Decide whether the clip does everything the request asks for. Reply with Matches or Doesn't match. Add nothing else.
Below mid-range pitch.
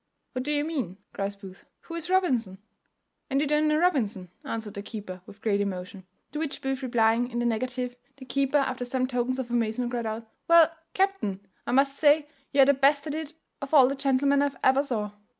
Doesn't match